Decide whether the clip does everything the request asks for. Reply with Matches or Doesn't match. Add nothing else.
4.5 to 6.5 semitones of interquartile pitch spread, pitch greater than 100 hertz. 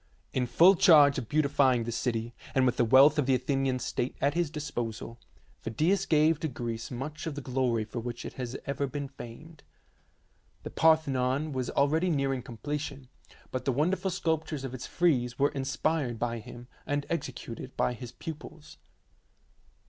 Doesn't match